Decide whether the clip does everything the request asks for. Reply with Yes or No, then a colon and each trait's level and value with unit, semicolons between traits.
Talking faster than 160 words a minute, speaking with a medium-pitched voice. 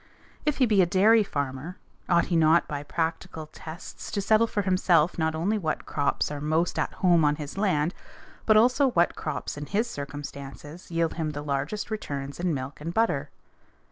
Yes: average, 185 wpm; medium, 165 Hz